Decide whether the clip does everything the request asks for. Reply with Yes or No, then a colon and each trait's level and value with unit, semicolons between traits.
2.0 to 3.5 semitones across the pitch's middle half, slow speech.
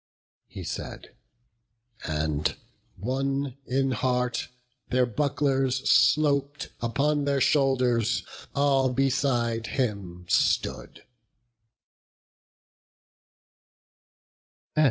Yes: average, 2.8 semitones; slow, 65 wpm